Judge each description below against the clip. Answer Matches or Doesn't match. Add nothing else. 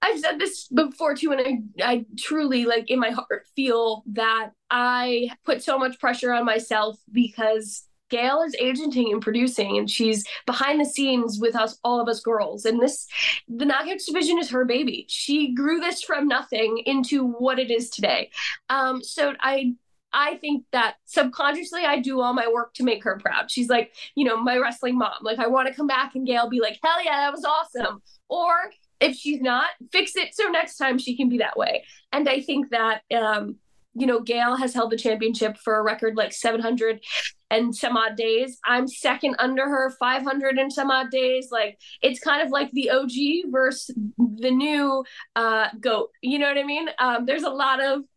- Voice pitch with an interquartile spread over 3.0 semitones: Matches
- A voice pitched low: Doesn't match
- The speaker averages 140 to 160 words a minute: Doesn't match